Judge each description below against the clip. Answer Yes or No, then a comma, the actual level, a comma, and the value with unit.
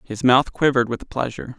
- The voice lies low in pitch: Yes, low, 125 Hz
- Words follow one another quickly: No, average, 190 wpm